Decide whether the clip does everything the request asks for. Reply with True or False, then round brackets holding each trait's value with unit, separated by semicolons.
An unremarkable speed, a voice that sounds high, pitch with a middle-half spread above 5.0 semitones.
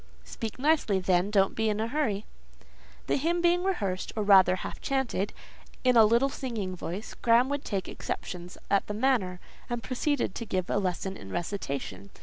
True (175 wpm; 210 Hz; 5.6 semitones)